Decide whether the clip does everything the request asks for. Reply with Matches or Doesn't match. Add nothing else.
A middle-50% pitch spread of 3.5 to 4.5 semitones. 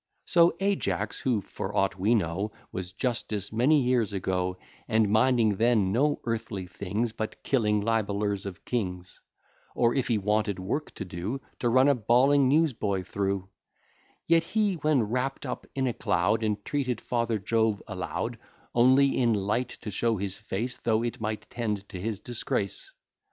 Matches